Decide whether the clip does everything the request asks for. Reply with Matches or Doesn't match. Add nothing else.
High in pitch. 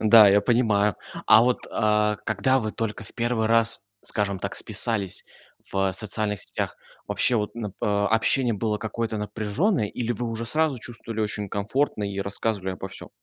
Doesn't match